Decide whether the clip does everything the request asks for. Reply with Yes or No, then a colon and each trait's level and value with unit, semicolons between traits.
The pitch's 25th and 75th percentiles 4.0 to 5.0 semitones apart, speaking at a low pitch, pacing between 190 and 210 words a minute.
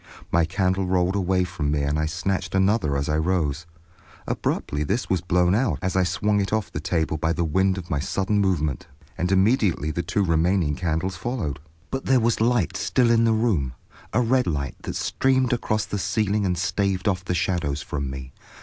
Yes: average, 4.5 semitones; very low, 90 Hz; average, 200 wpm